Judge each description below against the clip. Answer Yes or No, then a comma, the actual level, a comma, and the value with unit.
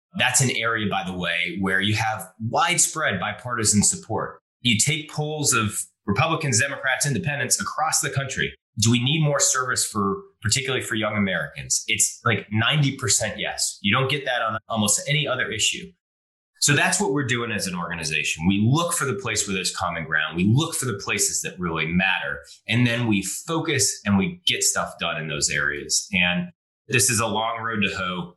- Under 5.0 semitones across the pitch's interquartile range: No, wide, 5.4 semitones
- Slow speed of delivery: No, average, 190 wpm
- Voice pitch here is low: Yes, low, 115 Hz